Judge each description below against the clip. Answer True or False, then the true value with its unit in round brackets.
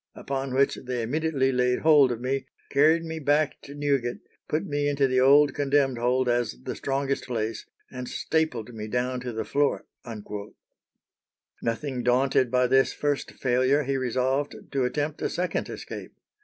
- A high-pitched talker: False (135 Hz)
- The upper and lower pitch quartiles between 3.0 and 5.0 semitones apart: False (2.5 semitones)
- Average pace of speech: True (160 wpm)